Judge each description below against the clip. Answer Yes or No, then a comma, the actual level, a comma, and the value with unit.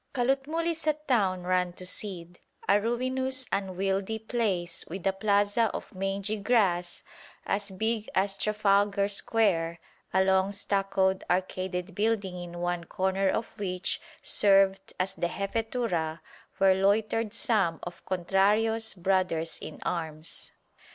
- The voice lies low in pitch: No, high, 195 Hz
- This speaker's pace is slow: Yes, slow, 125 wpm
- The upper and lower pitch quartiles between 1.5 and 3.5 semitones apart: Yes, average, 3.1 semitones